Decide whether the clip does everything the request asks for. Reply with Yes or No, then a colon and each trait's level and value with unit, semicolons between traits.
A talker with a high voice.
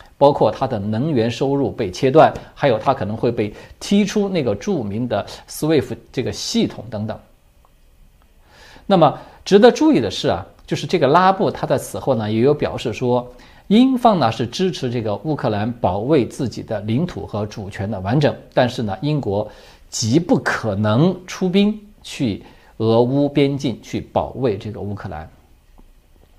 No: low, 120 Hz